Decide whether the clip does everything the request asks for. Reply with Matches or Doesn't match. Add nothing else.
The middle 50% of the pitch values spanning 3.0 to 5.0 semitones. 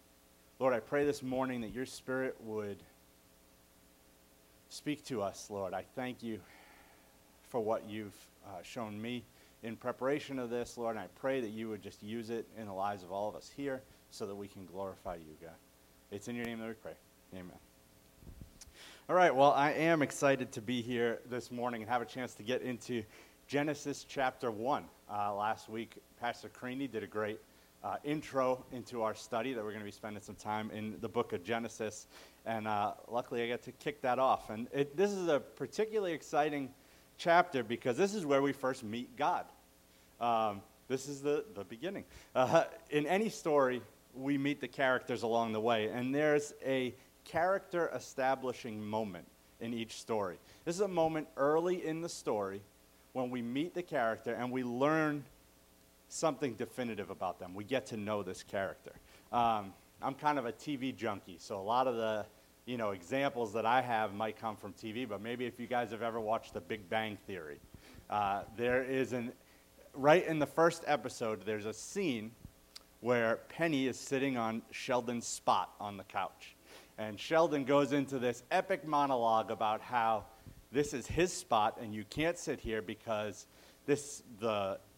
Matches